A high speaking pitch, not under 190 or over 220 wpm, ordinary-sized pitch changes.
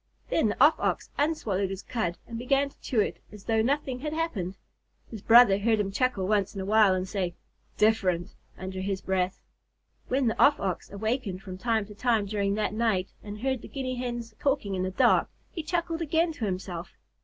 Yes: high, 215 Hz; average, 200 wpm; average, 4.8 semitones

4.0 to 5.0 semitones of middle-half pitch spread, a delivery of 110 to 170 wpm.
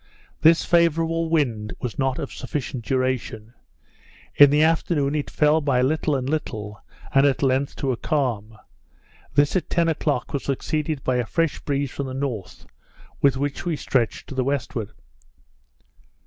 No: average, 3.1 semitones; average, 160 wpm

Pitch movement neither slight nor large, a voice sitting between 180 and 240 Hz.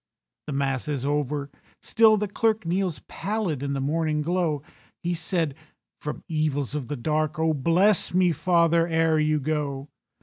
No: average, 3.2 semitones; medium, 155 Hz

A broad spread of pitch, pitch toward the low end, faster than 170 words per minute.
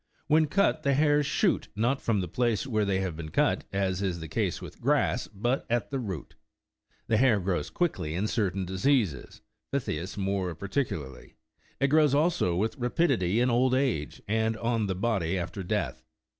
Yes: wide, 6.3 semitones; low, 110 Hz; average, 180 wpm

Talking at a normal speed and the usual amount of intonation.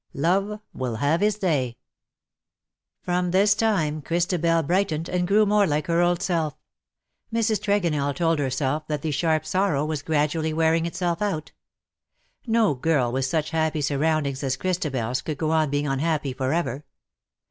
Yes: average, 150 wpm; average, 3.7 semitones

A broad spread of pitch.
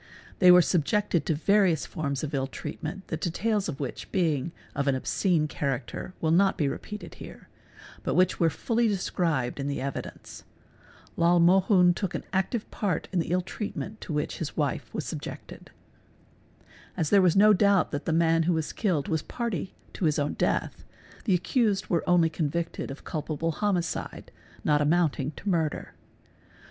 No: average, 4.2 semitones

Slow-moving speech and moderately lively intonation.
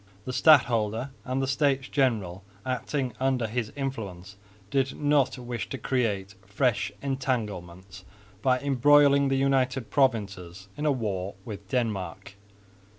Yes: slow, 125 wpm; average, 5.0 semitones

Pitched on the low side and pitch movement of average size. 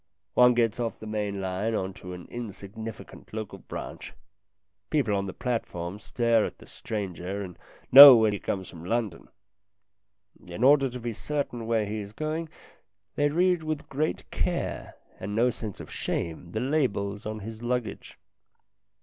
Yes: low, 110 Hz; average, 3.8 semitones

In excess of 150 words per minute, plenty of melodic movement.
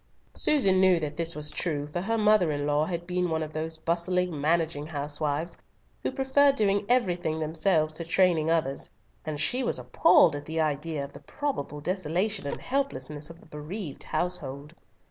No: average, 170 wpm; average, 3.8 semitones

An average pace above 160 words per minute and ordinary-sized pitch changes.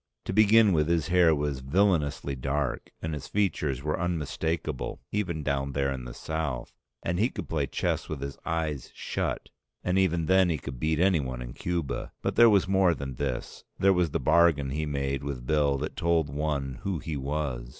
Yes: average, 190 wpm; average, 4.0 semitones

